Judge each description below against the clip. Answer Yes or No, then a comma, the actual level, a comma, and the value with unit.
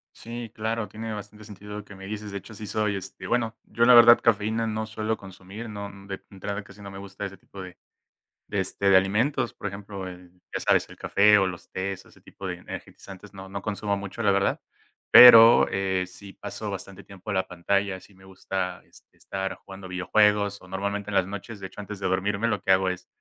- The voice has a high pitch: No, low, 100 Hz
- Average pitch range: No, narrow, 1.8 semitones